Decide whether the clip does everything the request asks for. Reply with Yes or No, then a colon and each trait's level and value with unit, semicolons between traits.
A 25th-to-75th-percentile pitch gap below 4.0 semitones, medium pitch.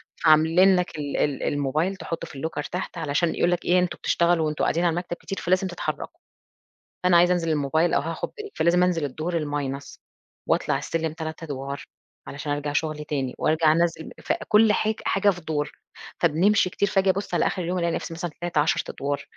Yes: average, 3.2 semitones; medium, 165 Hz